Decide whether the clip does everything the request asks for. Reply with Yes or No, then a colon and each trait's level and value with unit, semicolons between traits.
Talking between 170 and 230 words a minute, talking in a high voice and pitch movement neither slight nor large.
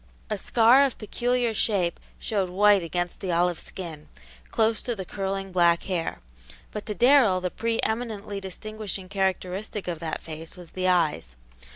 No: average, 160 wpm; high, 195 Hz; average, 3.6 semitones